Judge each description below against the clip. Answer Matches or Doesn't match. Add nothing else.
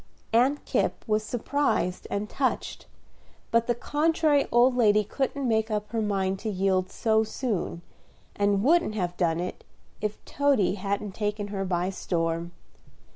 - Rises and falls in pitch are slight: Doesn't match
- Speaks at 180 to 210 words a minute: Doesn't match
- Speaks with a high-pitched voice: Matches